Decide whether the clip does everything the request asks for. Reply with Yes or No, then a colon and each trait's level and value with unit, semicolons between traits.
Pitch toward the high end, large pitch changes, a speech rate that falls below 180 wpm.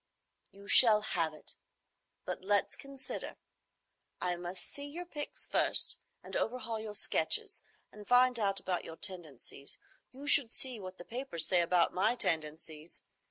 Yes: high, 205 Hz; wide, 6.3 semitones; average, 150 wpm